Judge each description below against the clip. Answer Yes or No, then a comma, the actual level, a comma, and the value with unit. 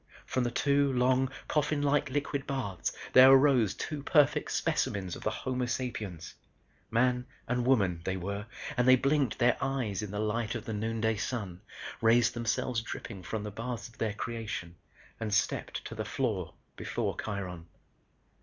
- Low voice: Yes, low, 115 Hz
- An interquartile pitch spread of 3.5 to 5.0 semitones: Yes, average, 3.9 semitones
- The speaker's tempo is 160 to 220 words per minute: Yes, average, 165 wpm